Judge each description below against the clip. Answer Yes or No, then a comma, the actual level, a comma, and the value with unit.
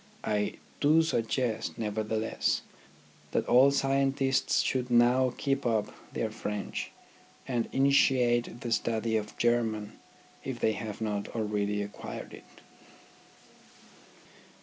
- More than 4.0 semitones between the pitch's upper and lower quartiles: No, average, 3.4 semitones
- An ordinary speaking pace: No, slow, 105 wpm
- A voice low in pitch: Yes, low, 115 Hz